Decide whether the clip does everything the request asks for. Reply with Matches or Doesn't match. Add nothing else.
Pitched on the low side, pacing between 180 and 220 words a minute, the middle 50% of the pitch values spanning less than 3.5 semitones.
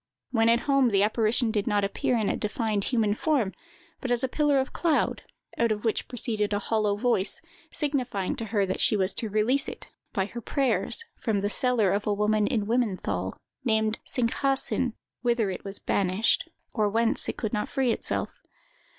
Doesn't match